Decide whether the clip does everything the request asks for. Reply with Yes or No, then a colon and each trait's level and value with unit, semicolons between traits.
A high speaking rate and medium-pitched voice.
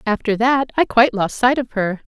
No: fast, 230 wpm; high, 235 Hz